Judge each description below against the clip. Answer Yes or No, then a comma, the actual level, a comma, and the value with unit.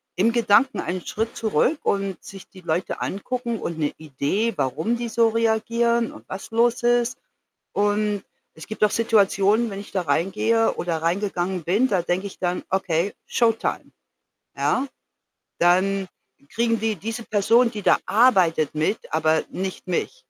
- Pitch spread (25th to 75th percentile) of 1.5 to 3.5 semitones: No, average, 4.2 semitones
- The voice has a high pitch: Yes, high, 205 Hz